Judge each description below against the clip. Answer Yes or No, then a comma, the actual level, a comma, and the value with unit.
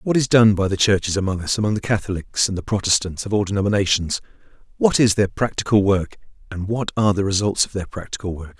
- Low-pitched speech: Yes, low, 100 Hz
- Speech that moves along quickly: Yes, fast, 210 wpm